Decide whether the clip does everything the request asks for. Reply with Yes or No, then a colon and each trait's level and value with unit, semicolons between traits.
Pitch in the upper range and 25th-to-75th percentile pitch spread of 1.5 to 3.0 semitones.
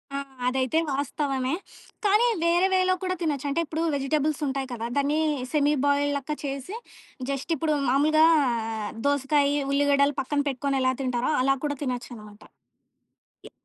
Yes: very high, 280 Hz; narrow, 2.4 semitones